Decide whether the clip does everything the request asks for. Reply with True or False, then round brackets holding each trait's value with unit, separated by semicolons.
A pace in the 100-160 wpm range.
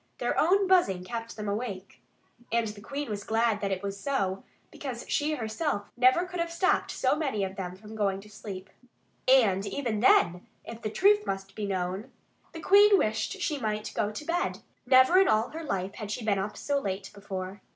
False (205 wpm)